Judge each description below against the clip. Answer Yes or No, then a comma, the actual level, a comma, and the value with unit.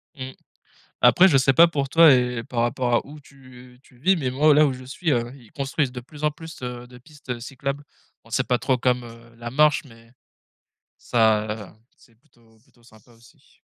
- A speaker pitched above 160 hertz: No, low, 125 Hz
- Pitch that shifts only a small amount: No, average, 3.2 semitones